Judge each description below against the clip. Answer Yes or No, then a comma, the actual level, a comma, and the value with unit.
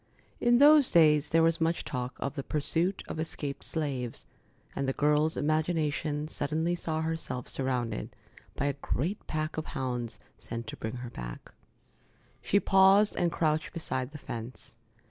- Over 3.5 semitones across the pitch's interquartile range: Yes, average, 4.0 semitones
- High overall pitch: No, medium, 150 Hz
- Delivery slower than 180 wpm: Yes, average, 155 wpm